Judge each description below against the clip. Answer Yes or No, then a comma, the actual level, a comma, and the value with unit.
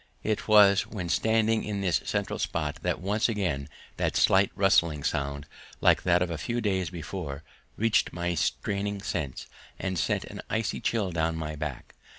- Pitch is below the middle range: Yes, very low, 95 Hz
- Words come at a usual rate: Yes, average, 165 wpm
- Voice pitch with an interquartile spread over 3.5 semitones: Yes, average, 4.2 semitones